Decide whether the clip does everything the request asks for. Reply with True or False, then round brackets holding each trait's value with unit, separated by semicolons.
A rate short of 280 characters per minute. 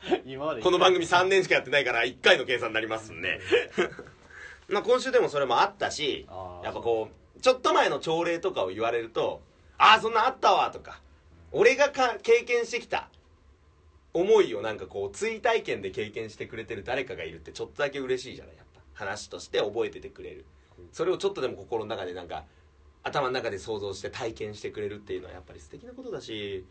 False (405 characters per minute)